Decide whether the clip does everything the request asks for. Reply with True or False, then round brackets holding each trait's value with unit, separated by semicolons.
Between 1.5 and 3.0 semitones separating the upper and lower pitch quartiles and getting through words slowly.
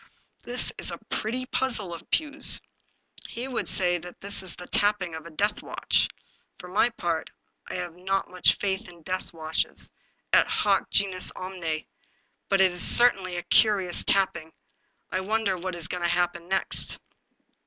False (2.7 semitones; 165 wpm)